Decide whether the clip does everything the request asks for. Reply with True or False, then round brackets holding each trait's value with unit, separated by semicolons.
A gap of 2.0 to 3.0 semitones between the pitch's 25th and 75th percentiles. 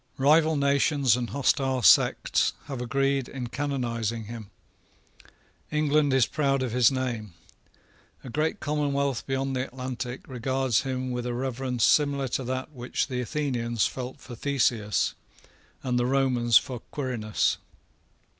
True (2.4 semitones)